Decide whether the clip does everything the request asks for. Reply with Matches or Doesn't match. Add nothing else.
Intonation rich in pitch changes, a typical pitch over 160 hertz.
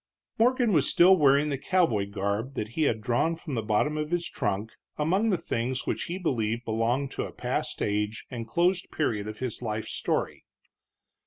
Doesn't match